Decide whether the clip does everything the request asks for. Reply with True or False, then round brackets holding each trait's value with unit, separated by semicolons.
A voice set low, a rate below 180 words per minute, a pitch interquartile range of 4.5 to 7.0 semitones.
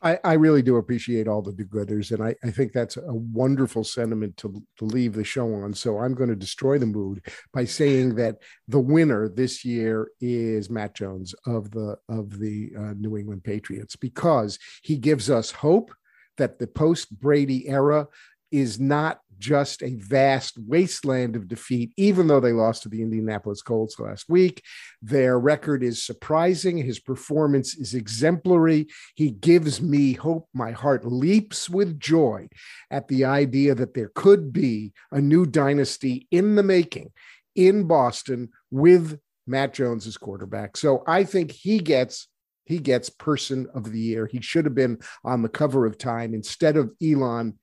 True (130 Hz; 170 wpm; 5.0 semitones)